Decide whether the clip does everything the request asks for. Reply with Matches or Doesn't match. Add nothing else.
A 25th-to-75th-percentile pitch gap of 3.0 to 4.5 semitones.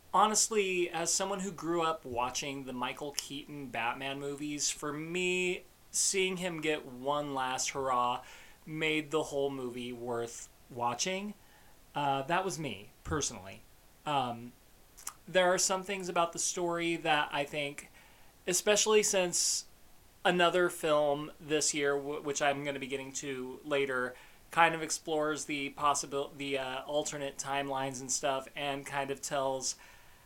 Matches